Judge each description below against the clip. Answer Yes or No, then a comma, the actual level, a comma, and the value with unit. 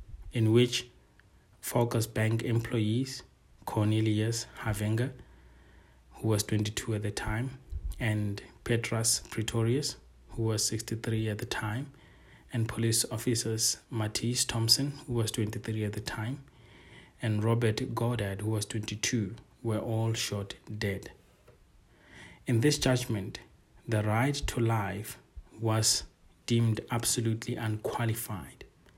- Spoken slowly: Yes, slow, 110 wpm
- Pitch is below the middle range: Yes, low, 115 Hz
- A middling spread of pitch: No, narrow, 1.7 semitones